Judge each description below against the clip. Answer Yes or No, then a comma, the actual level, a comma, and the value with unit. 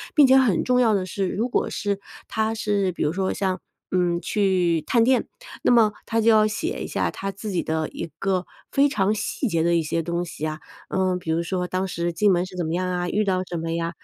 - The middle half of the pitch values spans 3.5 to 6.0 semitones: Yes, average, 3.8 semitones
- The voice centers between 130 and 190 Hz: Yes, medium, 185 Hz